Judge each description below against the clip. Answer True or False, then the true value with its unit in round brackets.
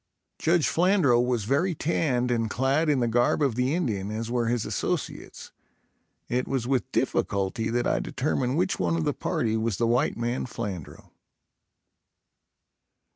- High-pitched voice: False (120 Hz)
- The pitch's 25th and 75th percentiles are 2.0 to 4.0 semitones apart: True (3.3 semitones)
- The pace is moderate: True (155 wpm)